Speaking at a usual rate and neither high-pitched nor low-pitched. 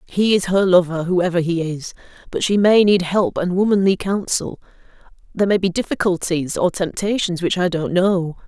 Yes: average, 170 wpm; medium, 180 Hz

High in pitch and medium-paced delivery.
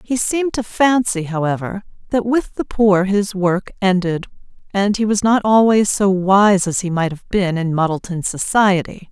Yes: high, 195 Hz; average, 180 wpm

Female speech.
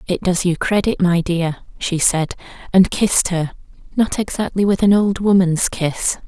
Yes: female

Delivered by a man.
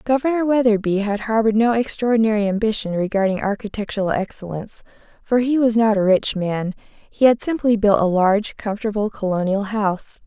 No: female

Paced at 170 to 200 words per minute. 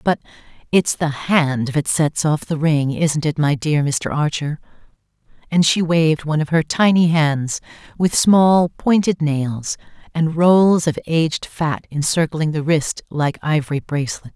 No: average, 160 wpm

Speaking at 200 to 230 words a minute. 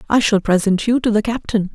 No: fast, 240 wpm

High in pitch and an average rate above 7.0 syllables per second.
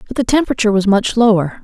Yes: high, 220 Hz; 7.5 syllables/s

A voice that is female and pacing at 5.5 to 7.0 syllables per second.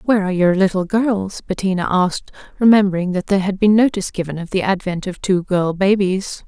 Yes: female; 6.0 syllables/s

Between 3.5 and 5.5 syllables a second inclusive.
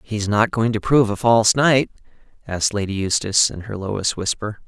No: 6.0 syllables/s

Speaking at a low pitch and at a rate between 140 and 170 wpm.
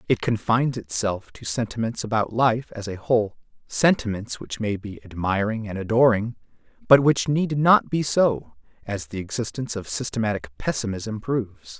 Yes: low, 110 Hz; average, 155 wpm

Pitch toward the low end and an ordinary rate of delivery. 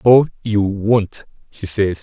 Yes: low, 105 Hz; average, 150 wpm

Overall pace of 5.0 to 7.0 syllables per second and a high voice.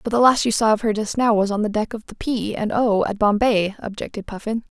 Yes: 5.8 syllables/s; high, 215 Hz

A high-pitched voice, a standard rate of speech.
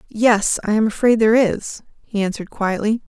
Yes: high, 215 Hz; average, 170 wpm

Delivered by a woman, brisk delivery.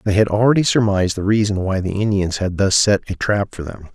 No: male; fast, 245 wpm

